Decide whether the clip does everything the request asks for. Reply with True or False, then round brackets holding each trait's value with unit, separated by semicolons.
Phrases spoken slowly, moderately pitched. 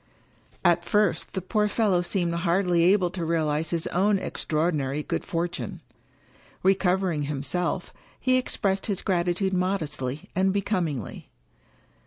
True (120 wpm; 175 Hz)